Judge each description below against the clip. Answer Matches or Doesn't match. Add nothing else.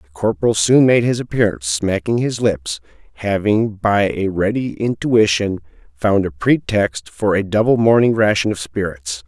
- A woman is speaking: Doesn't match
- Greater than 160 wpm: Doesn't match